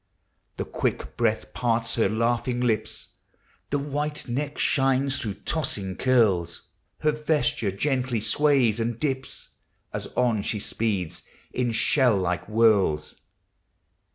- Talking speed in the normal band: No, slow, 120 wpm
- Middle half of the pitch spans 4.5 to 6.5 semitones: No, average, 3.9 semitones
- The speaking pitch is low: Yes, low, 120 Hz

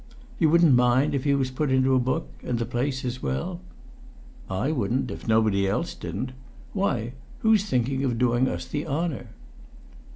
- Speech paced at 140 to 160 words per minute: No, average, 170 wpm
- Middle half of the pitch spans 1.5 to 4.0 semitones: Yes, average, 3.6 semitones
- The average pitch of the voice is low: Yes, low, 130 Hz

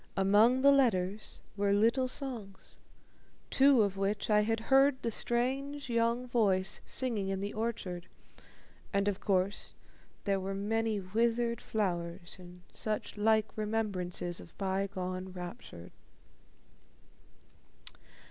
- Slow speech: Yes, slow, 115 wpm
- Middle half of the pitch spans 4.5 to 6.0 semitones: No, average, 3.5 semitones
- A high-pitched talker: Yes, high, 210 Hz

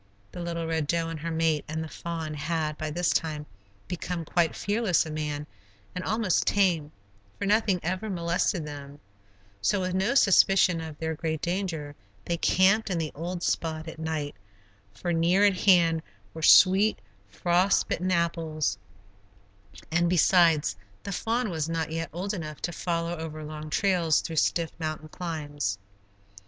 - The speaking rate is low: No, average, 160 wpm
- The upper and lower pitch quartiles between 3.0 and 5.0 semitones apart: No, narrow, 2.6 semitones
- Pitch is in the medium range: Yes, medium, 165 Hz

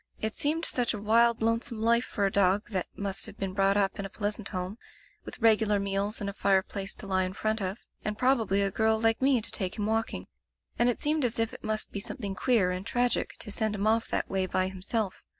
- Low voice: No, high, 210 Hz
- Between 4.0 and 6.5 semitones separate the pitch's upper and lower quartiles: No, narrow, 2.6 semitones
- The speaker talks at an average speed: No, fast, 240 wpm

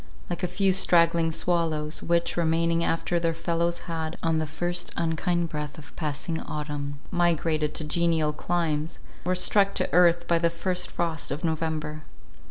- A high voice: No, medium, 165 Hz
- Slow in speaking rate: No, average, 160 wpm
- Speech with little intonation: Yes, narrow, 1.7 semitones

